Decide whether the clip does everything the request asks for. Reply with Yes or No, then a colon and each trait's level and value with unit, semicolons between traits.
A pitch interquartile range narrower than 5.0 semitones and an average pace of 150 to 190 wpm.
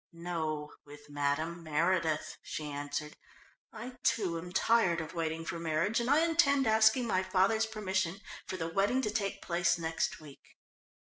No: wide, 5.5 semitones; average, 155 wpm